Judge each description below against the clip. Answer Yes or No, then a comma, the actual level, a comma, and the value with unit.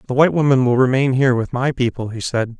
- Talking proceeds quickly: Yes, fast, 255 wpm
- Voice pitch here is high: No, low, 130 Hz